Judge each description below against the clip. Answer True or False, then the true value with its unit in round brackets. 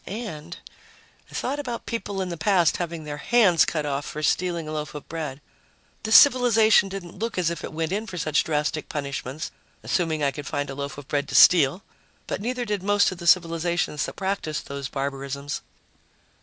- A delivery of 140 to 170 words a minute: False (195 wpm)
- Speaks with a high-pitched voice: False (165 Hz)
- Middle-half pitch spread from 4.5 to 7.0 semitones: True (4.9 semitones)